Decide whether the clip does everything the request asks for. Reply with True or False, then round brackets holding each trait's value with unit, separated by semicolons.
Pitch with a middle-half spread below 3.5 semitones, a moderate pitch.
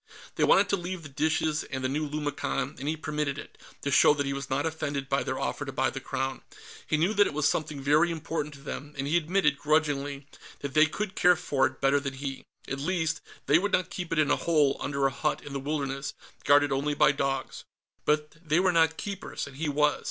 True (2.5 semitones; 150 Hz)